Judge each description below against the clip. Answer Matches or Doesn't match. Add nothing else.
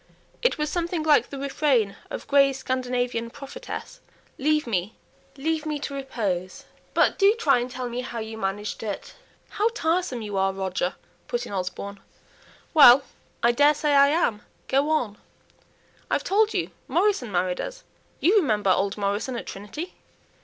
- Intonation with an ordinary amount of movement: Doesn't match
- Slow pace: Doesn't match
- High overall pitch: Matches